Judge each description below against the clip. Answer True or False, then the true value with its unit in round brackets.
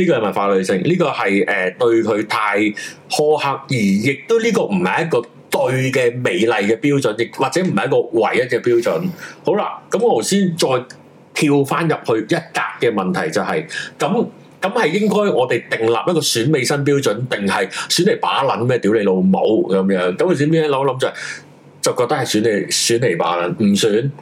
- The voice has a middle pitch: True (150 Hz)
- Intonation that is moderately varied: False (8.7 semitones)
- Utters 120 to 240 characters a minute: False (280 characters per minute)